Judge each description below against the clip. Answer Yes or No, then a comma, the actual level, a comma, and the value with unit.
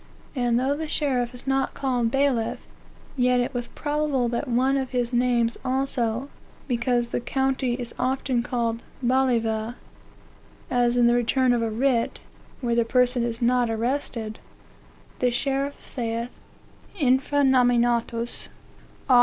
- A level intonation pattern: Yes, narrow, 2.0 semitones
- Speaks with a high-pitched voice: Yes, high, 245 Hz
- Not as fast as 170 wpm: Yes, average, 140 wpm